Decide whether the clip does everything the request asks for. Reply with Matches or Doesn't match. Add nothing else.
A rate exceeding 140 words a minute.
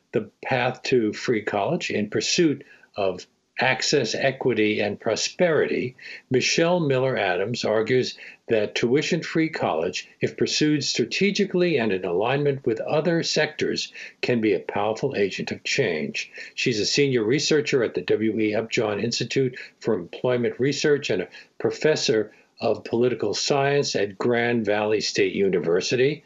Doesn't match